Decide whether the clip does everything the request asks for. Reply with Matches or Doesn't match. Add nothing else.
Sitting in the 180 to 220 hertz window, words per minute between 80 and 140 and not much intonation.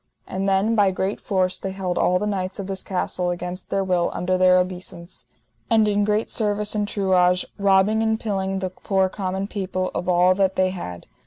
Doesn't match